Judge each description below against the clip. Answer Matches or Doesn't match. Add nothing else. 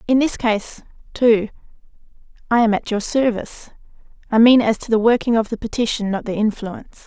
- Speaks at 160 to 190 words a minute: Matches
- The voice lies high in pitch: Matches